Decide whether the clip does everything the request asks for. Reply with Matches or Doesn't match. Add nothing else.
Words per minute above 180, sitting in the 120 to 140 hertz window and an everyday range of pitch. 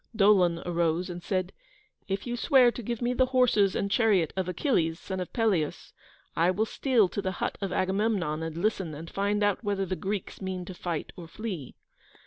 Doesn't match